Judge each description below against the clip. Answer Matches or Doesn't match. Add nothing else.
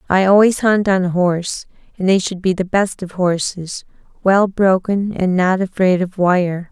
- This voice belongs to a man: Doesn't match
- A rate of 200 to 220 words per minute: Doesn't match